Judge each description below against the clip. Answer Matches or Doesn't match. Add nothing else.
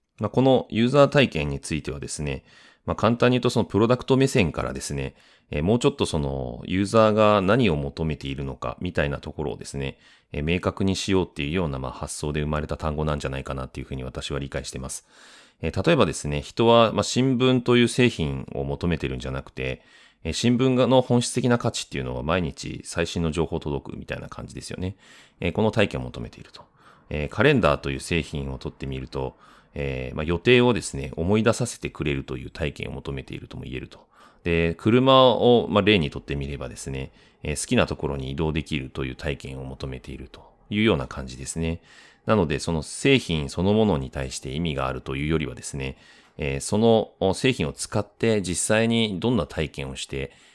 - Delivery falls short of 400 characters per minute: Doesn't match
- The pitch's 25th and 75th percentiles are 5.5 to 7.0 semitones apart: Doesn't match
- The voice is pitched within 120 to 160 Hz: Doesn't match